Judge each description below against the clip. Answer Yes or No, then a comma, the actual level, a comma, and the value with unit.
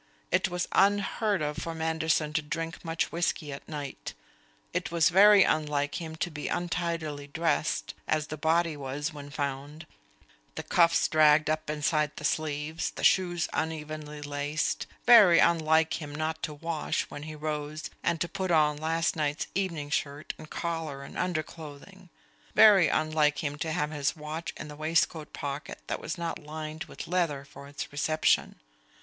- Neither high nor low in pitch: Yes, medium, 155 Hz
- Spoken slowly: No, average, 165 wpm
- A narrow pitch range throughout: Yes, narrow, 2.0 semitones